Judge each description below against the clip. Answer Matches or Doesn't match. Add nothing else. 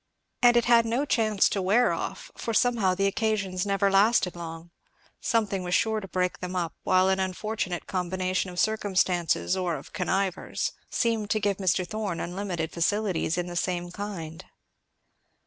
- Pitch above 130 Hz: Matches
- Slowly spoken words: Doesn't match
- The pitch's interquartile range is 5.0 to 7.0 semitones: Doesn't match